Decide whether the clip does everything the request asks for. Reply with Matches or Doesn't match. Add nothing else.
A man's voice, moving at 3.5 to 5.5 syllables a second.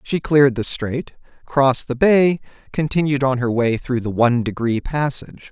Matches